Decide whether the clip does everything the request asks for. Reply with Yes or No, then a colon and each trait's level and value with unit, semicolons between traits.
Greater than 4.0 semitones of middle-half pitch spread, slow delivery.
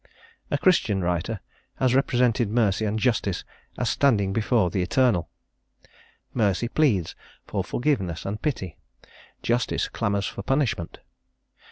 Yes: average, 4.4 semitones; slow, 120 wpm